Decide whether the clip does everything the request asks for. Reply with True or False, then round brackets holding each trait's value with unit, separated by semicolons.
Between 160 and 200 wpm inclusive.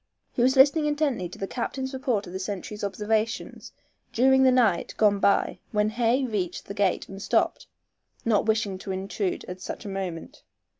True (180 wpm)